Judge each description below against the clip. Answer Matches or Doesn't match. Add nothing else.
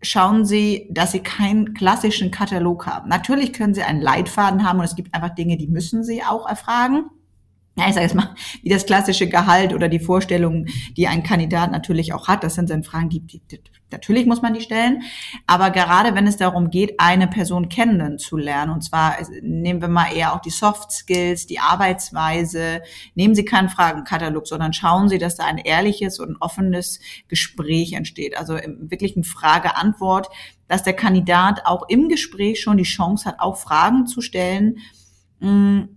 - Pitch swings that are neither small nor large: Matches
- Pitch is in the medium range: Matches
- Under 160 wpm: Doesn't match